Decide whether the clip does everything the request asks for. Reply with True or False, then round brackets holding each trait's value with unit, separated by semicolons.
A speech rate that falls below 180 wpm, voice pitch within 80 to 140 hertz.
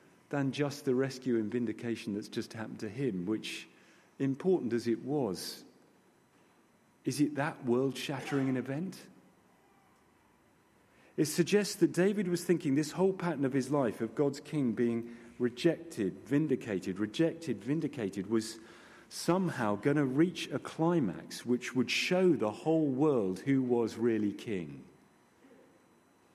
True (135 wpm; 135 Hz)